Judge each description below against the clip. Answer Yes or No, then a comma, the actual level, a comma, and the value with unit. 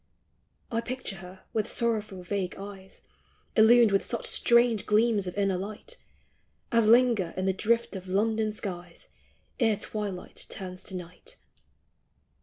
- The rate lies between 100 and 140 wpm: Yes, slow, 135 wpm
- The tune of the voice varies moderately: Yes, average, 3.4 semitones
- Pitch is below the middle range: No, high, 210 Hz